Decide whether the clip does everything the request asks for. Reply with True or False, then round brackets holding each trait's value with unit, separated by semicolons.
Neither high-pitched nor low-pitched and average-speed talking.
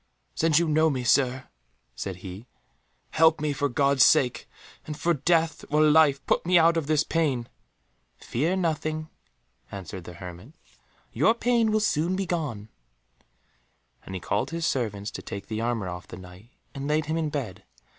True (145 Hz; 170 wpm)